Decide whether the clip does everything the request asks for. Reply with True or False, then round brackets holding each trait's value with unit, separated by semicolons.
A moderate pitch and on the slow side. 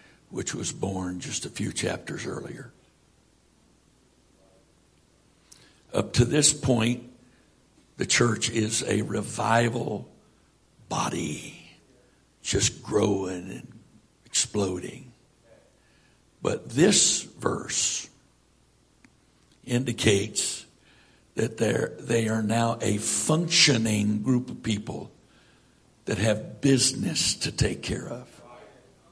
False (115 Hz; 85 wpm)